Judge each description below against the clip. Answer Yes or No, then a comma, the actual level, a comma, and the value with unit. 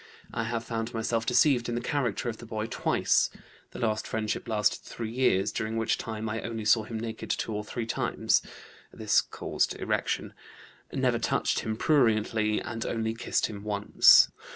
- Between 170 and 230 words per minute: Yes, average, 175 wpm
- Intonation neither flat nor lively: No, narrow, 1.4 semitones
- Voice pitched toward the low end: Yes, low, 115 Hz